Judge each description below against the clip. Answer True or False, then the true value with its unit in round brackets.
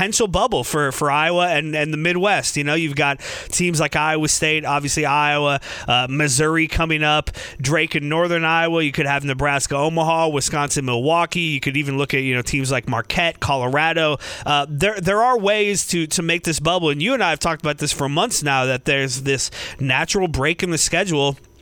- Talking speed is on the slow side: False (205 wpm)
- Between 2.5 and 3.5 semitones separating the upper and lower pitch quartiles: True (2.8 semitones)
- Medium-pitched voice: True (150 Hz)